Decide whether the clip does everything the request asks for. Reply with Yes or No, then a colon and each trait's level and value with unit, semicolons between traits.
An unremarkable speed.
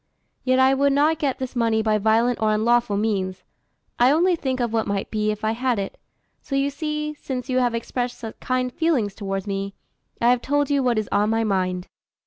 No: fast, 215 wpm